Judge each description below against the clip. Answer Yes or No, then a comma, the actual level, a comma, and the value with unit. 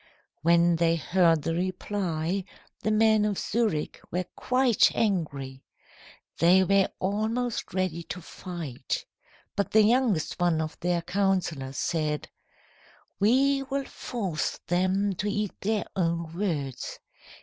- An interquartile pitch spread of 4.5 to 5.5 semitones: No, average, 4.0 semitones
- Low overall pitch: No, medium, 185 Hz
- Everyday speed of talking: No, slow, 120 wpm